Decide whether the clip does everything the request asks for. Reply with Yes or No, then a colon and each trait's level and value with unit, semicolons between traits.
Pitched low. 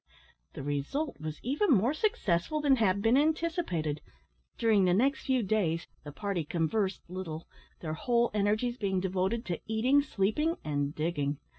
No: high, 200 Hz